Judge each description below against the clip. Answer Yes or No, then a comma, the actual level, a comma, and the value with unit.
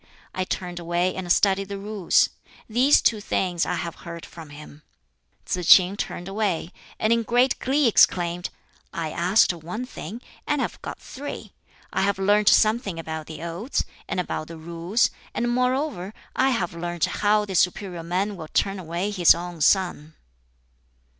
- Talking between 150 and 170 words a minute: Yes, average, 165 wpm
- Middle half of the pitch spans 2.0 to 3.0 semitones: No, average, 3.7 semitones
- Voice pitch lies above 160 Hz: Yes, medium, 185 Hz